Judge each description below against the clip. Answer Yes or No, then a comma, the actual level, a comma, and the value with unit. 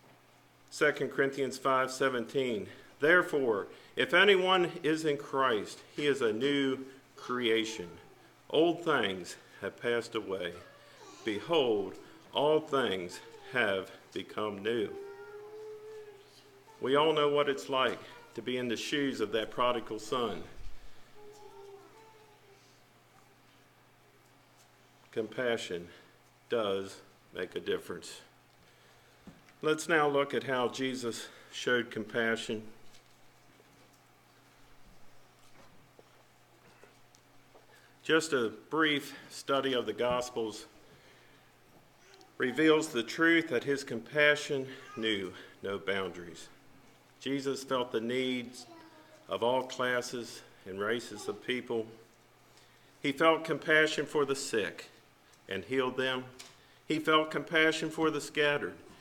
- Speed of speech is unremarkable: No, slow, 95 wpm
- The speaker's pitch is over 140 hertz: No, low, 135 Hz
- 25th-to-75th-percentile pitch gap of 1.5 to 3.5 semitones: No, average, 4.4 semitones